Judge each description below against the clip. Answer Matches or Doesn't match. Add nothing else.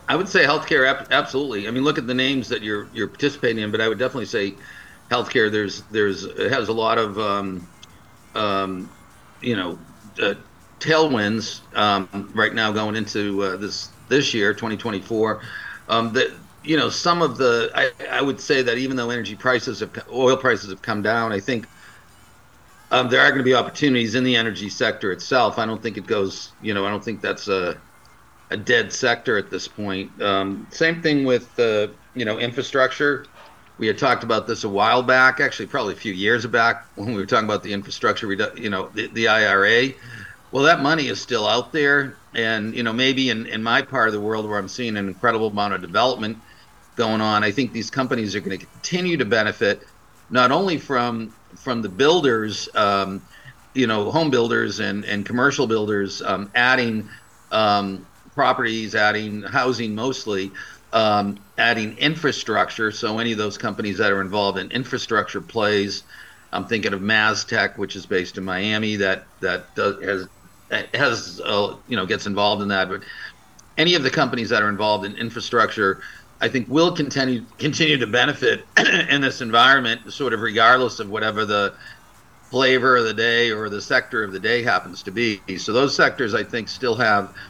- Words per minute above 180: Matches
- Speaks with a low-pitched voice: Matches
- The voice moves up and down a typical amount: Matches